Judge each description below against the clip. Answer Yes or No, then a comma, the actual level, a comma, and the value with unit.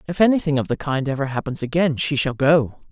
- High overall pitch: No, medium, 145 Hz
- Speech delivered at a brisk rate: Yes, fast, 225 wpm